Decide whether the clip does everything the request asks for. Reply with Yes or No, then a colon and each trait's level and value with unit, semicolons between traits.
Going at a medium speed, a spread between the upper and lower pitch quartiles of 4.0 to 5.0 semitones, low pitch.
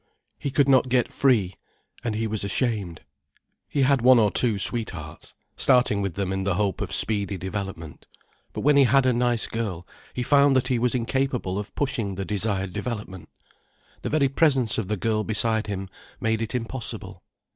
Yes: average, 180 wpm; average, 4.3 semitones; low, 110 Hz